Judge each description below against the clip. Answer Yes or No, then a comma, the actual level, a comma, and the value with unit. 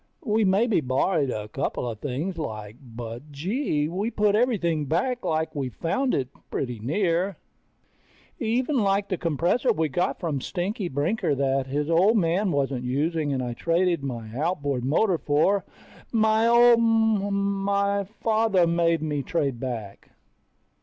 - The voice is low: No, medium, 170 Hz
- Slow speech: No, average, 145 wpm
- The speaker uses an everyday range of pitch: No, wide, 6.6 semitones